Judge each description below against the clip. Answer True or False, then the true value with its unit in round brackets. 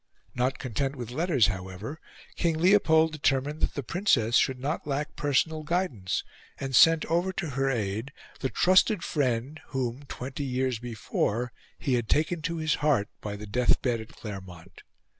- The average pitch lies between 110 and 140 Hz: True (135 Hz)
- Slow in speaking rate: False (160 wpm)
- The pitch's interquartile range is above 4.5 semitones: True (5.2 semitones)